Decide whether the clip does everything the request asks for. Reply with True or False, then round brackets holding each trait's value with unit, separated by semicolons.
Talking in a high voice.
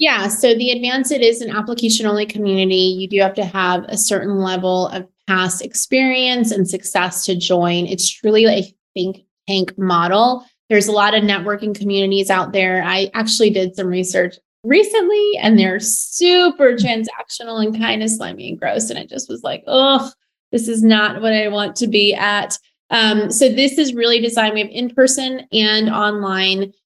True (210 Hz)